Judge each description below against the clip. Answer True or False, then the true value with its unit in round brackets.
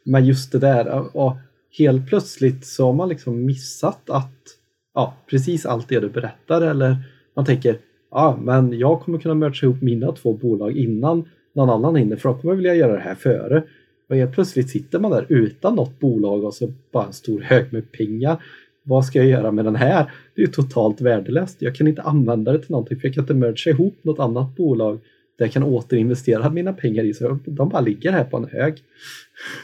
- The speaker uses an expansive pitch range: False (4.2 semitones)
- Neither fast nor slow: False (215 wpm)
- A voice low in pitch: True (130 Hz)